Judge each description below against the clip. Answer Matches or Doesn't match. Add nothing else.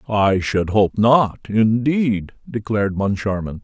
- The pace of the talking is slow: Matches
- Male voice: Matches